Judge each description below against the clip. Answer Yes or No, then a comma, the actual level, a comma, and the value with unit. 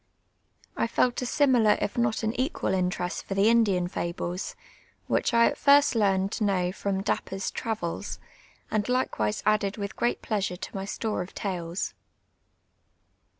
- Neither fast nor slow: Yes, average, 150 wpm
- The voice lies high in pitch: Yes, high, 205 Hz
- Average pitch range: Yes, average, 3.7 semitones